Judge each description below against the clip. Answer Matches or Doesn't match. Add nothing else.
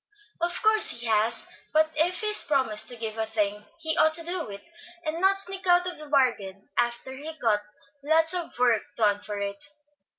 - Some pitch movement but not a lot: Doesn't match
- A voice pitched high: Matches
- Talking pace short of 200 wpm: Doesn't match